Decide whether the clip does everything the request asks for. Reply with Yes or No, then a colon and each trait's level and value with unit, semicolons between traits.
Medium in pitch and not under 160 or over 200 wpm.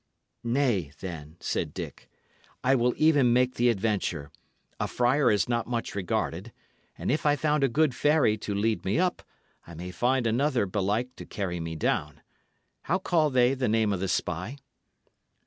No: low, 120 Hz; average, 170 wpm